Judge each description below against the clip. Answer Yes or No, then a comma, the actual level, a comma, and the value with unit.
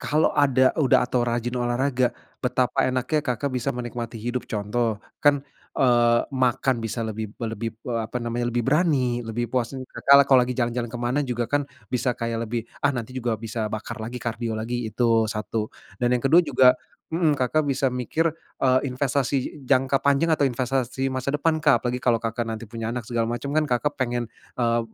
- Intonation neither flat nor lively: No, narrow, 2.2 semitones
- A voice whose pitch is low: Yes, low, 125 Hz